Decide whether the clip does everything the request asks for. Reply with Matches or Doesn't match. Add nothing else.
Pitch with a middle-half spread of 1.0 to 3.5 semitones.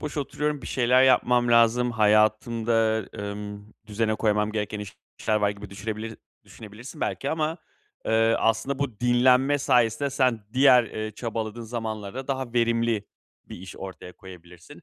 Matches